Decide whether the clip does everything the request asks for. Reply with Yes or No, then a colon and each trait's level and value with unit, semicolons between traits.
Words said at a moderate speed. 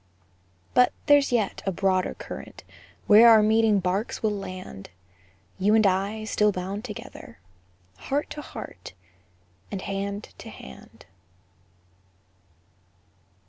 No: slow, 110 wpm